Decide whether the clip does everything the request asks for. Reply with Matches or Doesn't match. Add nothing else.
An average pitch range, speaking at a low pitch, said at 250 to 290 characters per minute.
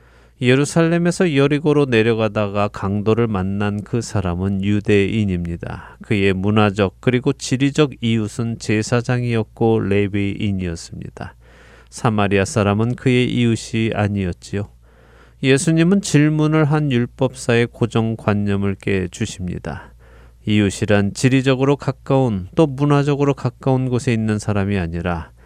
Doesn't match